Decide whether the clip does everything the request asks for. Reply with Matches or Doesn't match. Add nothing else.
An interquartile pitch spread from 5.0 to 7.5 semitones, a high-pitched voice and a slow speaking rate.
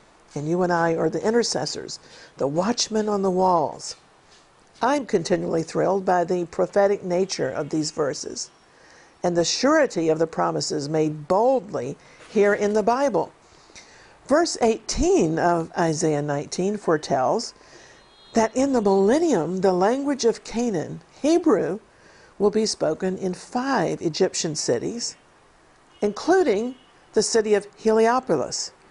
Matches